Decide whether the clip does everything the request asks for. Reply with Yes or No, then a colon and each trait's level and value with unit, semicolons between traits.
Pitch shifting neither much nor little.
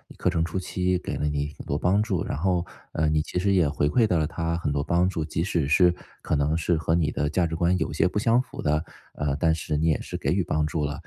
Yes: average, 3.0 semitones